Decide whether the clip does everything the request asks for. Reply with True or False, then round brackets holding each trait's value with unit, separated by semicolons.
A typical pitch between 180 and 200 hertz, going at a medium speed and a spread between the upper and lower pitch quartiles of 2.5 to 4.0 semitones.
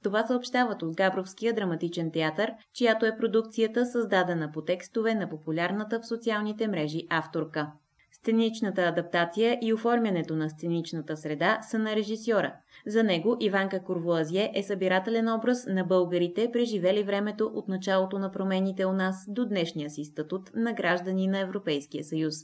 False (190 Hz; 145 wpm; 4.6 semitones)